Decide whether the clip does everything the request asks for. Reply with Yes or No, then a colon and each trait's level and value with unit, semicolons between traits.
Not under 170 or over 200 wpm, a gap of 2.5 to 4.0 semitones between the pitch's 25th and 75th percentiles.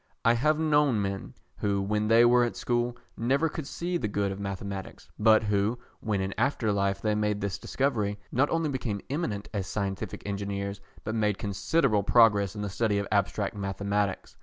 Yes: average, 185 wpm; average, 3.2 semitones